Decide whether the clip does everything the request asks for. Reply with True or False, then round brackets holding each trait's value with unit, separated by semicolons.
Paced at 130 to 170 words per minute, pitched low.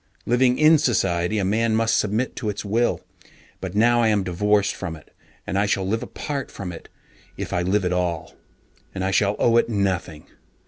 False (195 wpm; 105 Hz)